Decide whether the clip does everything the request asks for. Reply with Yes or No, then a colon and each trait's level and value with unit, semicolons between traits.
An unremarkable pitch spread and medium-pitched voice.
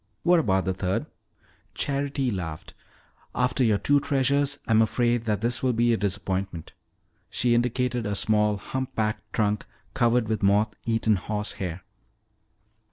No: average, 3.6 semitones; low, 110 Hz